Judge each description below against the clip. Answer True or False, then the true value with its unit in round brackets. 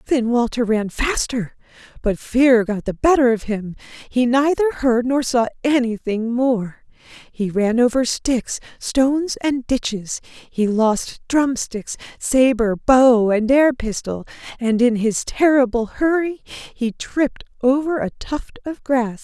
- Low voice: False (245 Hz)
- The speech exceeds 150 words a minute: False (145 wpm)